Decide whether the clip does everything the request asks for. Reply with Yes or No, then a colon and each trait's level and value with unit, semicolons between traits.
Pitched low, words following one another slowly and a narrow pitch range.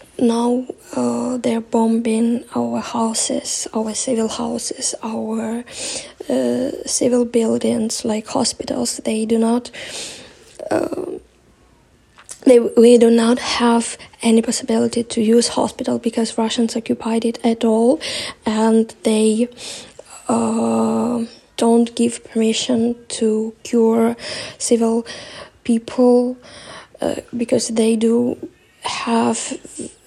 No: high, 235 Hz; slow, 100 wpm; narrow, 1.5 semitones